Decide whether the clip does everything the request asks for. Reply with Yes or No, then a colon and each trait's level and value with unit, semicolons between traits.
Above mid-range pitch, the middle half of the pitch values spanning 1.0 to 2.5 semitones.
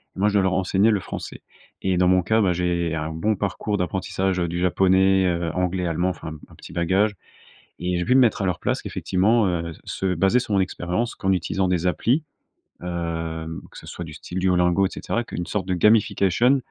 No: very low, 90 Hz; narrow, 2.0 semitones